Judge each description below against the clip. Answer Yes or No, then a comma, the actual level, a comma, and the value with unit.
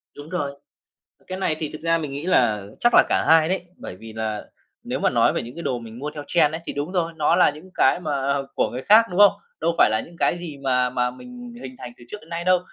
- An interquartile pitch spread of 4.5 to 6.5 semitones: Yes, wide, 5.6 semitones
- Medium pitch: Yes, medium, 155 Hz